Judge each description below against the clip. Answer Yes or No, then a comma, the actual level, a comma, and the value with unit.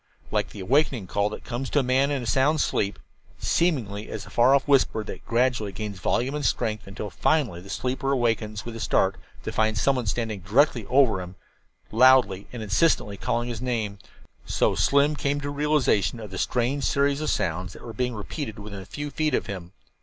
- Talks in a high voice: No, low, 120 Hz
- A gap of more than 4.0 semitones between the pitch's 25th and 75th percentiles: Yes, average, 5.0 semitones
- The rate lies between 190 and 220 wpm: Yes, fast, 205 wpm